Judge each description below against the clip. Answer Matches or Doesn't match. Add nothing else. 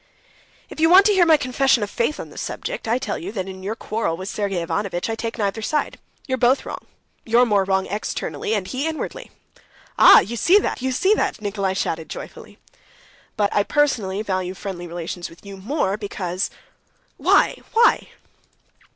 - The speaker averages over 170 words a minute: Matches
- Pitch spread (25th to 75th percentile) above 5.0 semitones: Matches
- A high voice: Matches